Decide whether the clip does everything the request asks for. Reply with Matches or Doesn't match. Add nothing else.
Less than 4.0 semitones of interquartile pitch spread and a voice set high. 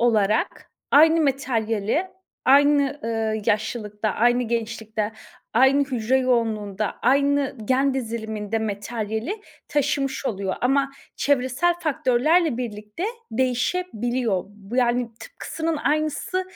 Doesn't match